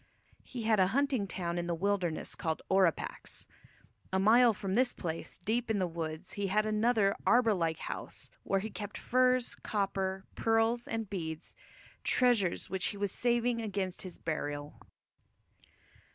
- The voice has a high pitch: Yes, high, 200 Hz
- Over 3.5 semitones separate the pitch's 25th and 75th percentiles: Yes, average, 4.0 semitones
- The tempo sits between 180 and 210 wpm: No, average, 150 wpm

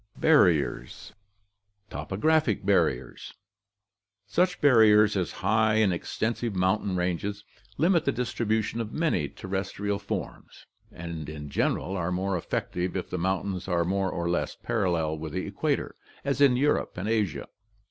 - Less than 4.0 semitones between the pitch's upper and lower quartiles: Yes, average, 3.6 semitones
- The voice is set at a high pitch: No, low, 100 Hz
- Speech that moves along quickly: No, average, 140 wpm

